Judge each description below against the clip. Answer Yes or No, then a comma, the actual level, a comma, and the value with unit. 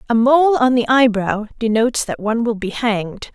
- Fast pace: No, average, 195 wpm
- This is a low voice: No, high, 235 Hz